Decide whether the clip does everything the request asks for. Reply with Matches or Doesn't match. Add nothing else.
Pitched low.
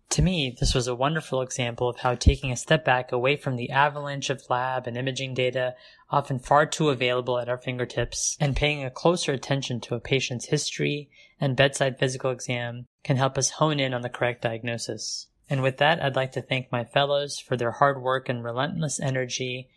Matches